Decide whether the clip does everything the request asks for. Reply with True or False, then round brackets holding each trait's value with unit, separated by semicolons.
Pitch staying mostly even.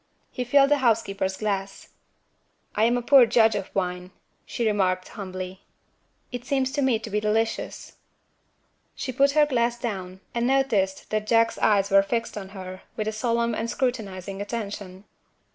False (3.7 semitones)